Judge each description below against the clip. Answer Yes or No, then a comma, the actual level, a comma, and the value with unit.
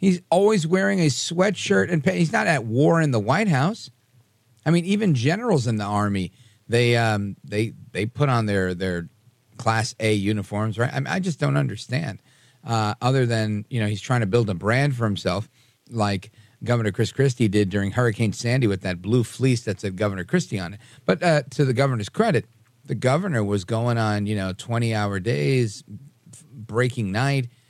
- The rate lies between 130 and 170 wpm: No, average, 195 wpm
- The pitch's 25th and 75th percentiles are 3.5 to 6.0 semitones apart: Yes, average, 4.7 semitones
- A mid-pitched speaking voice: No, low, 120 Hz